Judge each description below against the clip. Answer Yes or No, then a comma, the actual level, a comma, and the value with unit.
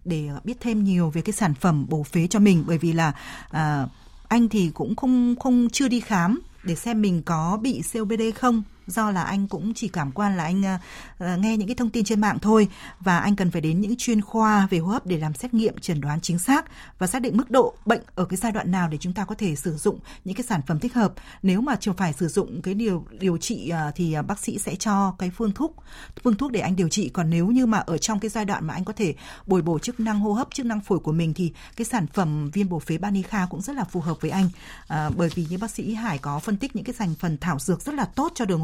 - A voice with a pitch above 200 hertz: No, high, 195 Hz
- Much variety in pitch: No, average, 4.6 semitones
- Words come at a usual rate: No, fast, 270 wpm